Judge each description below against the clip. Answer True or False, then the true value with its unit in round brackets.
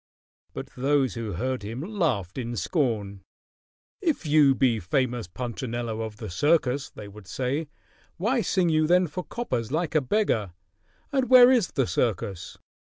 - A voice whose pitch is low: True (130 Hz)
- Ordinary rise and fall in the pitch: False (6.8 semitones)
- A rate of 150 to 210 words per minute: True (155 wpm)